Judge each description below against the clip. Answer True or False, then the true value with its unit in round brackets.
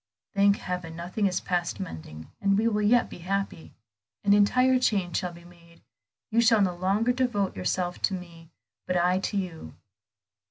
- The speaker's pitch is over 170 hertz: True (185 Hz)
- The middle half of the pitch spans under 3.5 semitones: True (3.0 semitones)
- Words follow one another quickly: False (170 wpm)